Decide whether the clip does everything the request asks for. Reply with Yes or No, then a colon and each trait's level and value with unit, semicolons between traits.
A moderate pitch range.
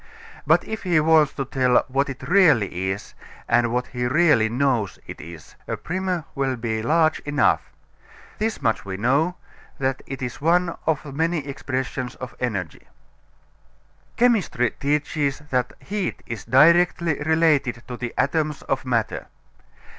Yes: average, 4.7 semitones